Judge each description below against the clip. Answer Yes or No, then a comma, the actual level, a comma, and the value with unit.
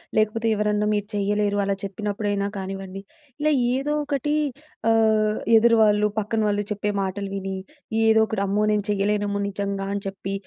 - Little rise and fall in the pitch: Yes, narrow, 1.5 semitones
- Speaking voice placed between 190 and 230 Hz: Yes, high, 205 Hz